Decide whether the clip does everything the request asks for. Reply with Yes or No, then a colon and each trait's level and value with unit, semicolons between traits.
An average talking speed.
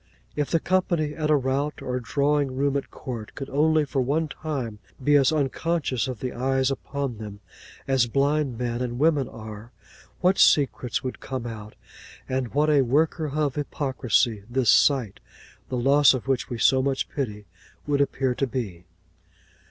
Yes: average, 170 wpm